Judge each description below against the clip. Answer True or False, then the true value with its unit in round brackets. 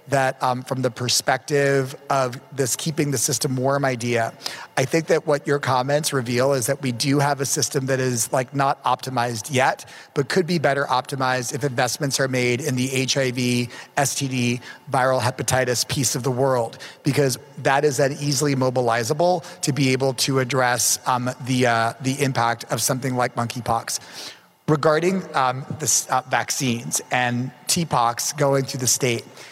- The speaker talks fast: False (165 wpm)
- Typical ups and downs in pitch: False (2.2 semitones)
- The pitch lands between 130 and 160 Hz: True (135 Hz)